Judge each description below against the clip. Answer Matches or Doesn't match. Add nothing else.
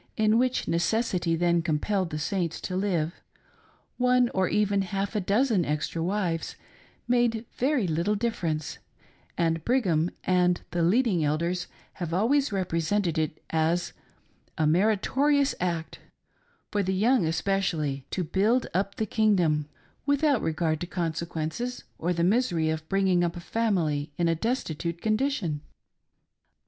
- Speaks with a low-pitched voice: Doesn't match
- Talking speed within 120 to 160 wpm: Matches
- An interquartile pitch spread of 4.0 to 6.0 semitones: Matches